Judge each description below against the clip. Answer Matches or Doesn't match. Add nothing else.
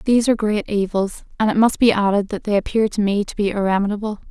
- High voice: Matches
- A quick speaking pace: Matches